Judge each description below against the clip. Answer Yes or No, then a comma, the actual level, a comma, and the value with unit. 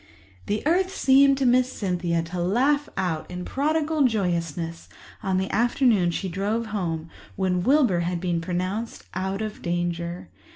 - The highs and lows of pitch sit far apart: Yes, wide, 6.0 semitones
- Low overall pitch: No, high, 190 Hz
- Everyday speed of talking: Yes, average, 150 wpm